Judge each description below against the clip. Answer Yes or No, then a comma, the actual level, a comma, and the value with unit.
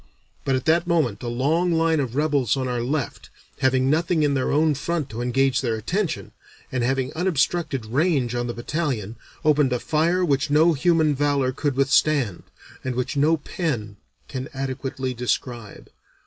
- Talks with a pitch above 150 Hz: No, low, 135 Hz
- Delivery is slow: No, average, 165 wpm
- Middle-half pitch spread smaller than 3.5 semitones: No, average, 3.8 semitones